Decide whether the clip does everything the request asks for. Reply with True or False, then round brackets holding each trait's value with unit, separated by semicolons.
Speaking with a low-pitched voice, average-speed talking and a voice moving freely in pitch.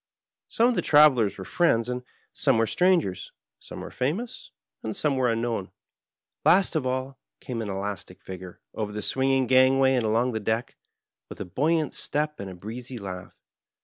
False (125 Hz; 175 wpm; 4.4 semitones)